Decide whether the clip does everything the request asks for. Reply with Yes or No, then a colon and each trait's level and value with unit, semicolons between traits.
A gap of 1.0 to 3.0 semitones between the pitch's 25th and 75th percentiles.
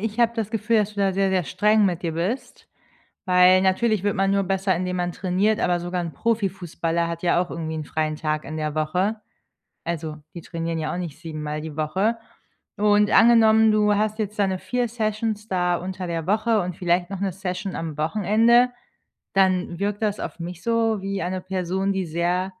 No: average, 3.7 semitones